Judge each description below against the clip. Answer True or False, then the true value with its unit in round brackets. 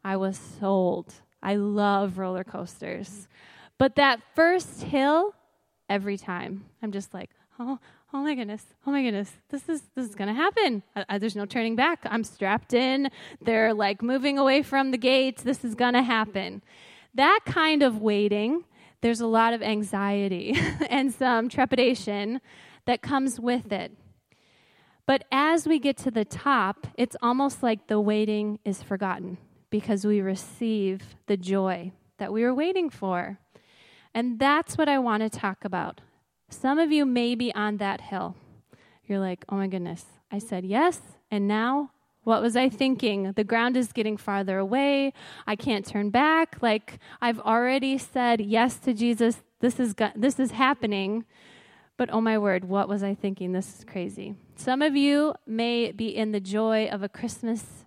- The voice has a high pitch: True (225 Hz)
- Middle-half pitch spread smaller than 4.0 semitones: False (4.7 semitones)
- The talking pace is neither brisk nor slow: True (170 wpm)